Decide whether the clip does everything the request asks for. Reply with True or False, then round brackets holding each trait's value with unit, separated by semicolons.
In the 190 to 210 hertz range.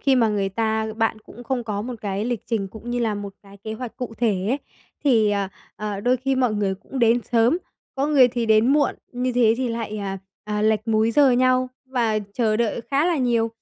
False (230 Hz)